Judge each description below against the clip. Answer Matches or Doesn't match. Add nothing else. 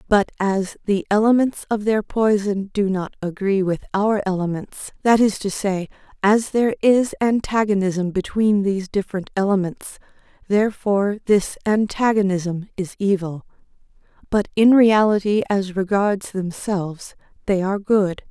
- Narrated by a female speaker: Matches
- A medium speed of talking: Doesn't match